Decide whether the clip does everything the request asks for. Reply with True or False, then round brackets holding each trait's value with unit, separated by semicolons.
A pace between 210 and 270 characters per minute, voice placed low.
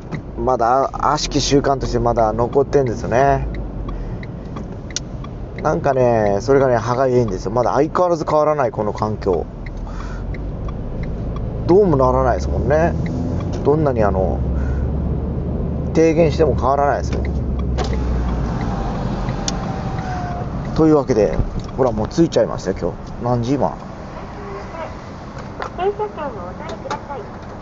True (250 characters per minute; 120 Hz)